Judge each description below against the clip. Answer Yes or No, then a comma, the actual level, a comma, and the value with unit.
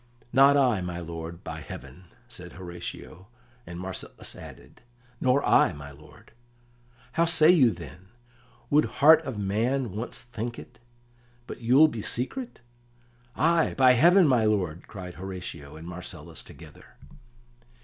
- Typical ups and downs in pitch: No, wide, 7.5 semitones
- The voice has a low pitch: Yes, low, 100 Hz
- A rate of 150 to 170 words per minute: No, slow, 135 wpm